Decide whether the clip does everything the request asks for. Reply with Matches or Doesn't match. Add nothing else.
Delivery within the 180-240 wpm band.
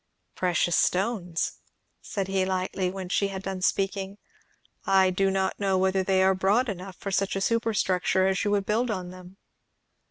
Doesn't match